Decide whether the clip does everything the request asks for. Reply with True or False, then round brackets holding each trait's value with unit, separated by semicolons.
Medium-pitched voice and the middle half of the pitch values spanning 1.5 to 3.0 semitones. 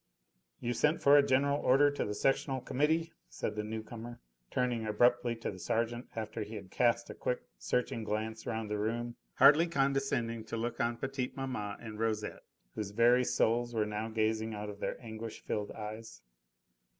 False (115 Hz; 2.6 semitones)